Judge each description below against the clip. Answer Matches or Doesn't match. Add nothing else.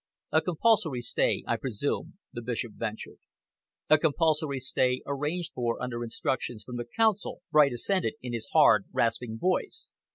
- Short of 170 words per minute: Matches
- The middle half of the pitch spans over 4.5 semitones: Matches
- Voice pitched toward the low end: Matches